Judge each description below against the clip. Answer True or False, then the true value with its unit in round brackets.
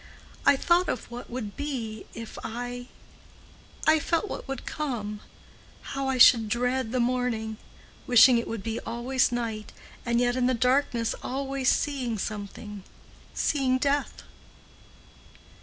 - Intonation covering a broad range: False (2.8 semitones)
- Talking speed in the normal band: False (115 wpm)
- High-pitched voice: True (245 Hz)